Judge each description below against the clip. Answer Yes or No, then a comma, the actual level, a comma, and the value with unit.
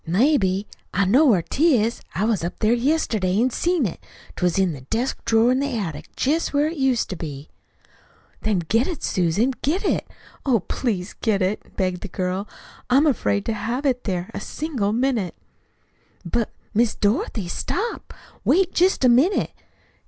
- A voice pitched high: Yes, high, 225 Hz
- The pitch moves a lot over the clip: Yes, wide, 6.1 semitones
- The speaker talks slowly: No, average, 175 wpm